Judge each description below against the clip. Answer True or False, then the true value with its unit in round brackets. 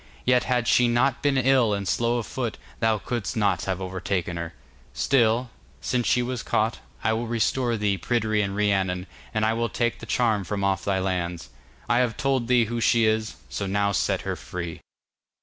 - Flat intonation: False (3.6 semitones)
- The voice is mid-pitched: False (110 Hz)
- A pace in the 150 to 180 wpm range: False (190 wpm)